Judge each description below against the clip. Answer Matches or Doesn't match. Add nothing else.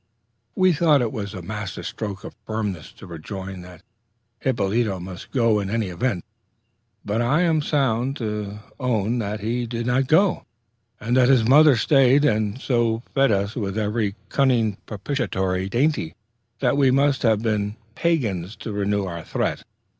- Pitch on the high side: Doesn't match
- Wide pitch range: Doesn't match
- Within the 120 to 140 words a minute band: Doesn't match